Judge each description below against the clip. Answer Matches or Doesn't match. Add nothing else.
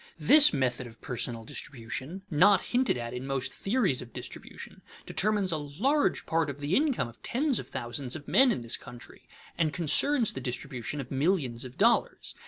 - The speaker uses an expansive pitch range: Matches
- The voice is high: Doesn't match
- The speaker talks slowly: Doesn't match